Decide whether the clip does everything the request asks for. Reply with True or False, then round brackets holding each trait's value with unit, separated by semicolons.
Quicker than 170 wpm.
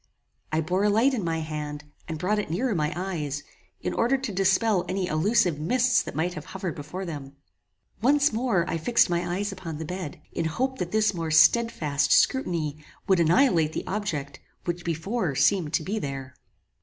True (185 wpm)